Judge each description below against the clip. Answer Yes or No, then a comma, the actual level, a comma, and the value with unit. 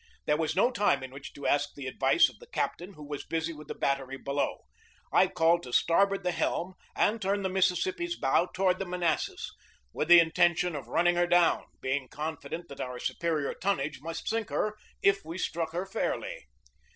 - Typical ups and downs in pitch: Yes, average, 4.5 semitones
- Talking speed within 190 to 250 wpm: Yes, average, 200 wpm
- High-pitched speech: No, medium, 170 Hz